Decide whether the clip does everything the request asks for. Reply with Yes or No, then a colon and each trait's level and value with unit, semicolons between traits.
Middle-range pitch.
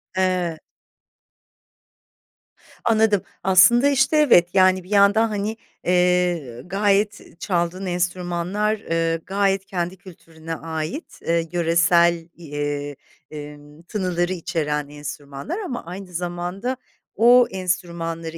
Yes: medium, 180 Hz